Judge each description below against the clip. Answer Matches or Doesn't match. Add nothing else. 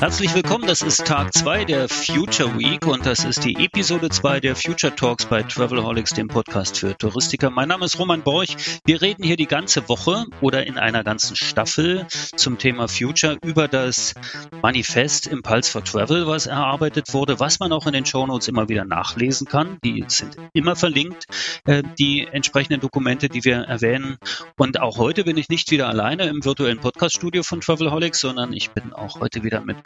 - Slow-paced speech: Doesn't match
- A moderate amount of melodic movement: Matches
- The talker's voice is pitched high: Doesn't match